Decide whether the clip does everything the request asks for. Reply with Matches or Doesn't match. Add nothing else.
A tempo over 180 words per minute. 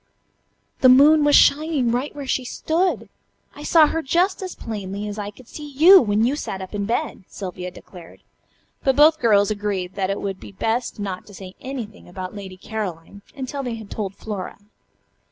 Matches